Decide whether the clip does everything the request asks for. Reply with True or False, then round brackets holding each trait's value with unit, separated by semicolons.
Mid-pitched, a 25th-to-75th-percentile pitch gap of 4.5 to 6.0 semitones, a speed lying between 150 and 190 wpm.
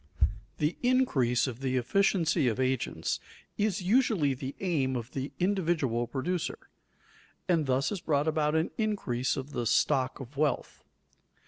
False (145 Hz; 5.5 semitones; 140 wpm)